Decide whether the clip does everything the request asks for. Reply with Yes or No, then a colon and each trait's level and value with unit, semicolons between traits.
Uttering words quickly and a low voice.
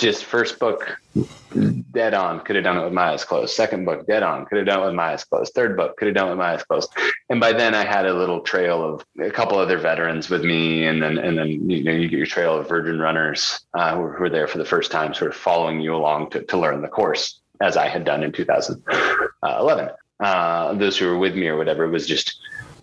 Yes: fast, 260 wpm; very low, 85 Hz